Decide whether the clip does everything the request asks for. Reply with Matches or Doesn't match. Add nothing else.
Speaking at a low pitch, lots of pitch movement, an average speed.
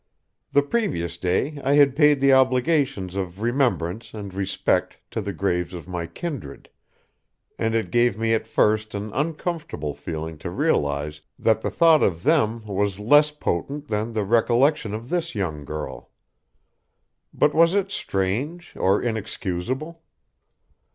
Matches